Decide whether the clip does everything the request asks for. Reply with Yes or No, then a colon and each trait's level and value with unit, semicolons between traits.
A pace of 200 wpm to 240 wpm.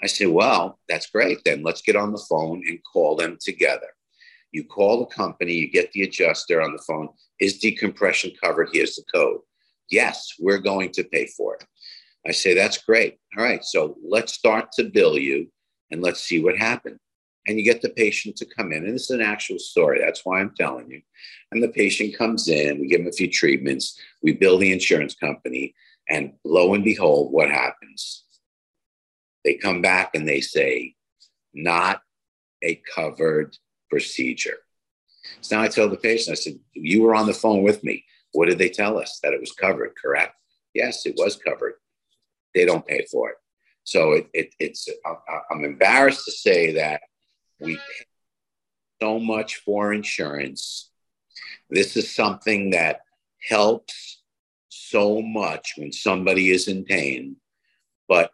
No: average, 175 wpm